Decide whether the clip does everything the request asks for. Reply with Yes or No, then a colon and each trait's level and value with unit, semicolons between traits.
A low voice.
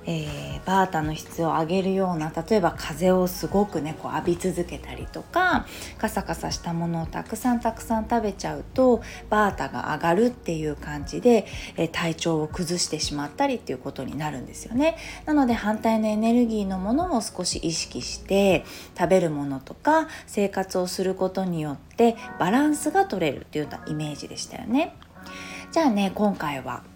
No: high, 190 Hz